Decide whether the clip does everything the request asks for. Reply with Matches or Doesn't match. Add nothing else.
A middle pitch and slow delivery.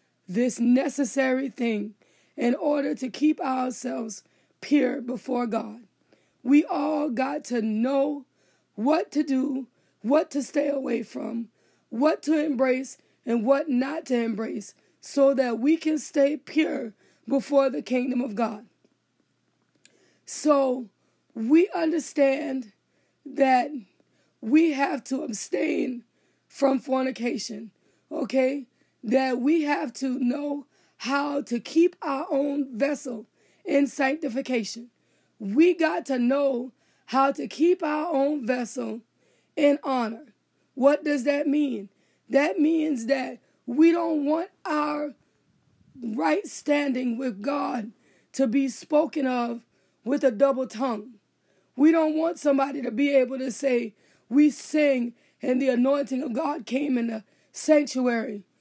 Doesn't match